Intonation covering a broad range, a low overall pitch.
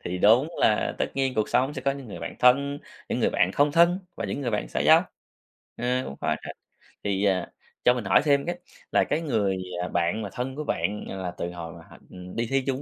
Yes: wide, 6.3 semitones; low, 115 Hz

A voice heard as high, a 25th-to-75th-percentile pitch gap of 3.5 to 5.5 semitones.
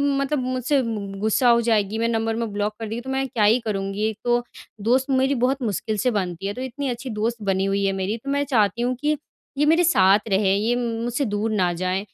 Yes: high, 225 Hz; average, 3.9 semitones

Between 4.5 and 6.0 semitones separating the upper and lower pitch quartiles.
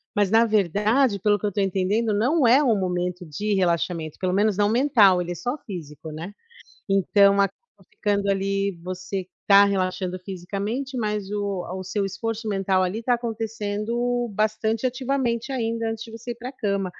No: average, 3.3 semitones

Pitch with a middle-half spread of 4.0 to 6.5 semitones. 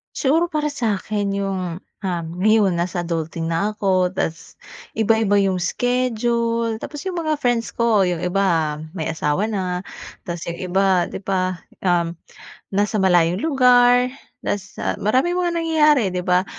Yes: average, 5.3 semitones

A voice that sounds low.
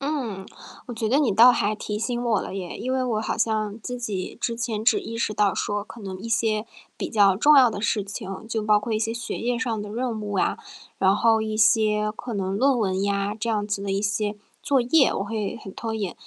No: high, 215 Hz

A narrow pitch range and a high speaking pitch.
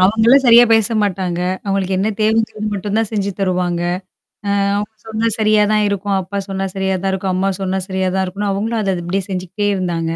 Yes: narrow, 2.2 semitones; high, 195 Hz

